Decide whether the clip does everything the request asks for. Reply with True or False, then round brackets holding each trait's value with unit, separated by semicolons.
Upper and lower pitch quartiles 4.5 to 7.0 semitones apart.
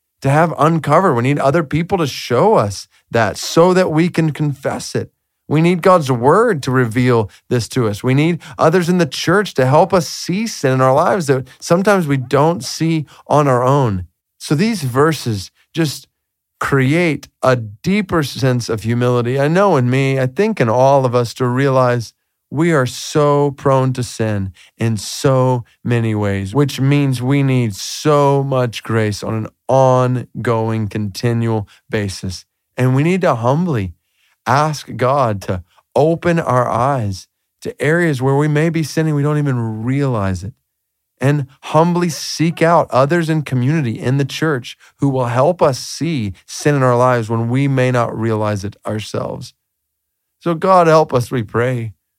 True (5.0 semitones)